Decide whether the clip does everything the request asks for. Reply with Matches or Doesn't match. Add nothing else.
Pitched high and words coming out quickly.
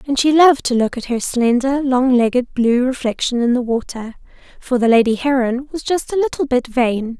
Matches